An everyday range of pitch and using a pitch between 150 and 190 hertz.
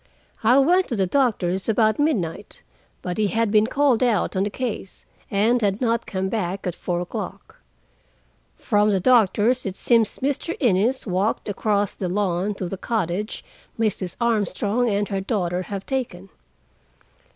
No: average, 3.8 semitones; high, 210 Hz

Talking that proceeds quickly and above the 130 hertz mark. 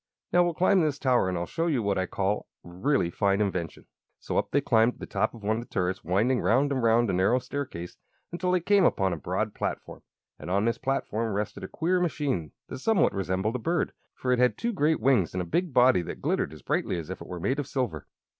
No: fast, 250 wpm; low, 115 Hz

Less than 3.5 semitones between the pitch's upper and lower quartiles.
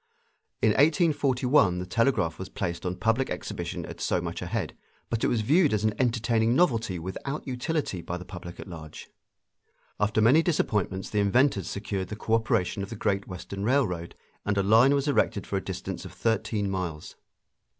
No: average, 5.2 semitones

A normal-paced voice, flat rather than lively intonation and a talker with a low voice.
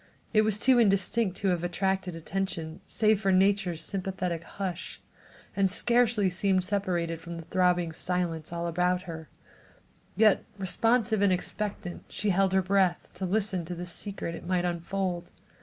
No: average, 155 wpm; narrow, 2.3 semitones; medium, 185 Hz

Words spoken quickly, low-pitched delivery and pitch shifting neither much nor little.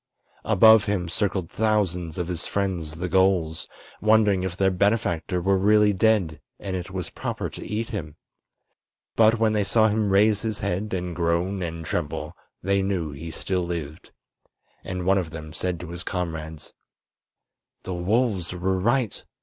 No: average, 160 wpm; very low, 95 Hz; average, 3.3 semitones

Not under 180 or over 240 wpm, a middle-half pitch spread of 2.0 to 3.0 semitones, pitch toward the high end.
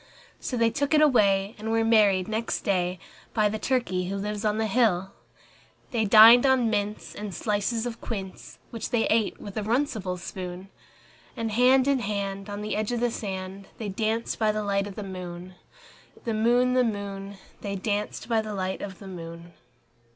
Yes: average, 190 wpm; average, 2.7 semitones; high, 210 Hz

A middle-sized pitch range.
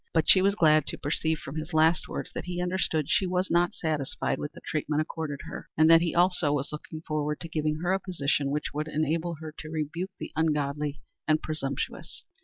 No: narrow, 2.1 semitones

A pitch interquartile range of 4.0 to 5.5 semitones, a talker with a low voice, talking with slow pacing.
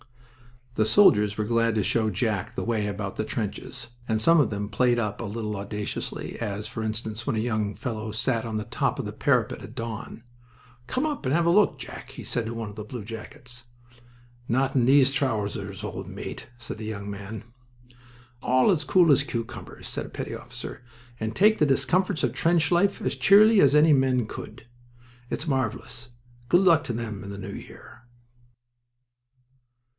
No: average, 4.4 semitones; low, 115 Hz; average, 185 wpm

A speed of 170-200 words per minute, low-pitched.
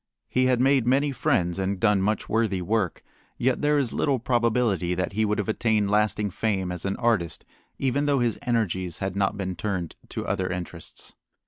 Yes: average, 190 wpm; low, 105 Hz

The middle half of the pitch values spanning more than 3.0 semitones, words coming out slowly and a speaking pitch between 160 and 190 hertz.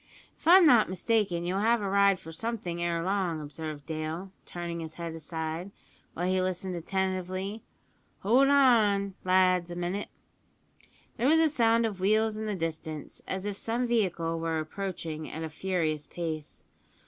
No: average, 4.1 semitones; average, 160 wpm; medium, 185 Hz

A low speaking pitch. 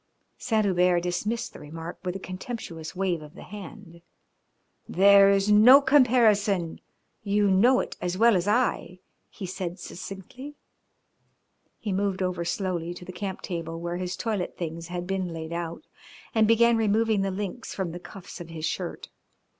No: high, 190 Hz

